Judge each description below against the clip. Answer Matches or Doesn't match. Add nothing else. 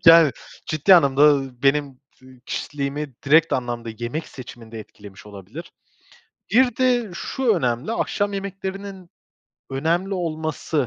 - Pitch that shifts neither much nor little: Doesn't match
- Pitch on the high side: Doesn't match